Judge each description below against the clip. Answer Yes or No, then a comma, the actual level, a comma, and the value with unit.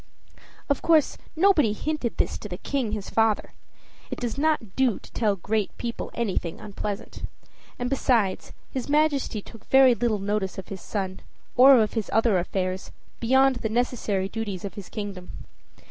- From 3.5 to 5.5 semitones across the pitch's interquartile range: Yes, average, 4.6 semitones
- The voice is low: No, high, 225 Hz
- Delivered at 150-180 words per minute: Yes, average, 160 wpm